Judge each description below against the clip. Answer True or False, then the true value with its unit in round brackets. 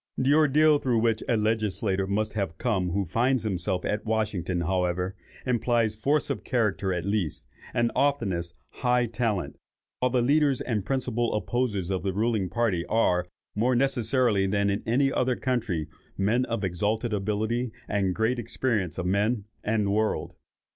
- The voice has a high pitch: False (110 Hz)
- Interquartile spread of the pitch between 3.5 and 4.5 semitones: True (4.0 semitones)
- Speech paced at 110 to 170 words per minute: True (160 wpm)